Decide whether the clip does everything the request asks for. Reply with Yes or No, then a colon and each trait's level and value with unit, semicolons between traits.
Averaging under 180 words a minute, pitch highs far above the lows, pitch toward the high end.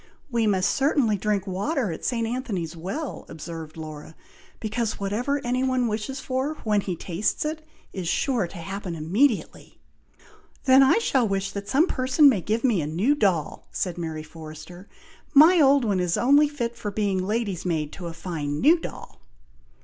Yes: average, 170 wpm; wide, 6.9 semitones; high, 205 Hz